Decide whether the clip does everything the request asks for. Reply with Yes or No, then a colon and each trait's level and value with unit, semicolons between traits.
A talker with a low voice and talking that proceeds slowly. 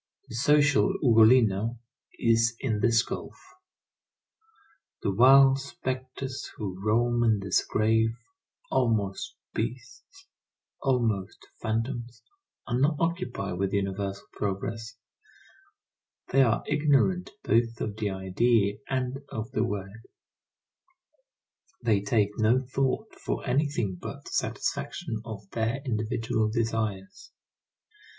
Yes: low, 115 Hz; slow, 105 wpm